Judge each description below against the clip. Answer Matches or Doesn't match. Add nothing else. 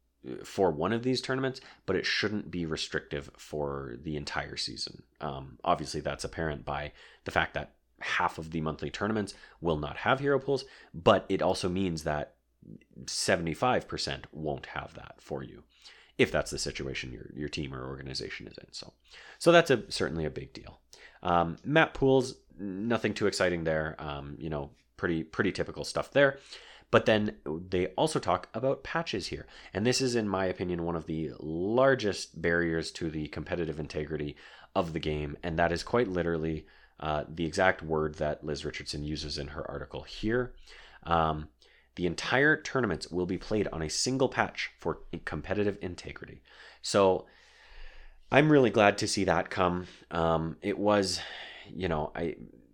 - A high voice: Doesn't match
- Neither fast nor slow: Matches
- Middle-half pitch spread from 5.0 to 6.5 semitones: Matches